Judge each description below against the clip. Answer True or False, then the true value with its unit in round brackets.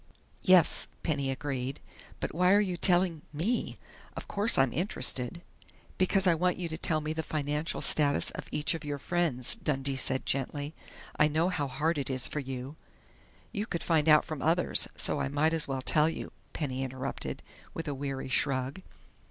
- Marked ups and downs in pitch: False (3.9 semitones)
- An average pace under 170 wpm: False (185 wpm)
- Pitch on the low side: False (150 Hz)